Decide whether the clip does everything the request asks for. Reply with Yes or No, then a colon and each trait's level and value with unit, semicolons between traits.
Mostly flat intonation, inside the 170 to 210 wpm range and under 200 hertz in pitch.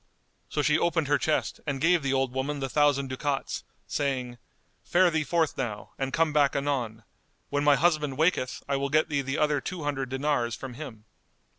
Yes: narrow, 2.3 semitones; average, 190 wpm; medium, 140 Hz